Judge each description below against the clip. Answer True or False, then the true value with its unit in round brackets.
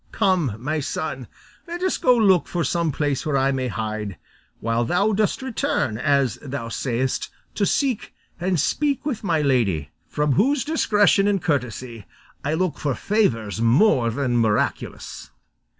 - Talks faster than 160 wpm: False (150 wpm)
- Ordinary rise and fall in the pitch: False (8.8 semitones)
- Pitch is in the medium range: True (145 Hz)